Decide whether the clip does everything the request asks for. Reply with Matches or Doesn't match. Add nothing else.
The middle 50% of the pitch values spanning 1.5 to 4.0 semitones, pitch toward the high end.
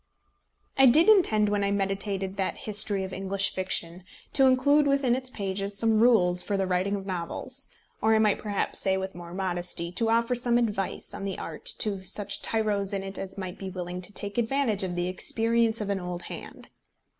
Matches